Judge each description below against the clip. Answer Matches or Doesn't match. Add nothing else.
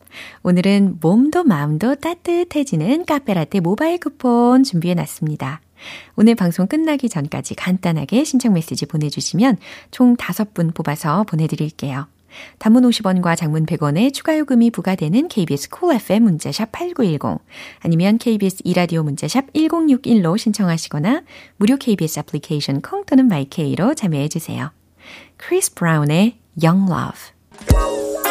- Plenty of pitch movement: Matches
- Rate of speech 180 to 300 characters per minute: Doesn't match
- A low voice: Doesn't match